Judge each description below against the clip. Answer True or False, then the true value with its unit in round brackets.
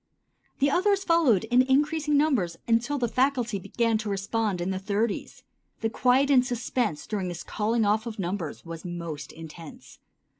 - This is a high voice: True (225 Hz)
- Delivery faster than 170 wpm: False (160 wpm)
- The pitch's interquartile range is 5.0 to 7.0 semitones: True (5.6 semitones)